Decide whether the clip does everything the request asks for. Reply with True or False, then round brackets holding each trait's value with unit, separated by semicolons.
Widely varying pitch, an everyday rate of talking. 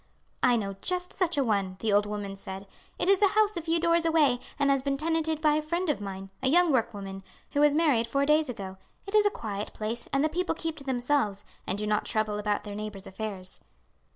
False (7.7 semitones; 235 wpm)